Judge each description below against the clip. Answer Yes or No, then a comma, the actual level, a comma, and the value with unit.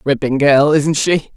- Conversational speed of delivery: Yes, average, 175 wpm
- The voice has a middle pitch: Yes, medium, 145 Hz